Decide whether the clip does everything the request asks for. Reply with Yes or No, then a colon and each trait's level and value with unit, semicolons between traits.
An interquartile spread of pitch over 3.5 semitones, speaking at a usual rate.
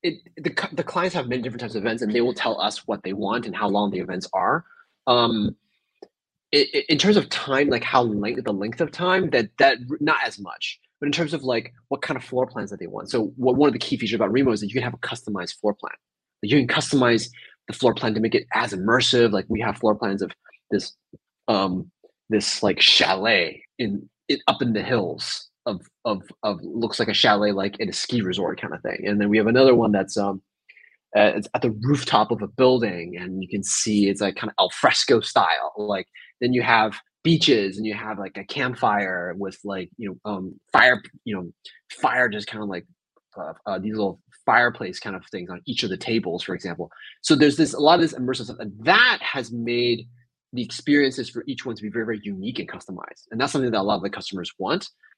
No: average, 3.9 semitones; fast, 240 wpm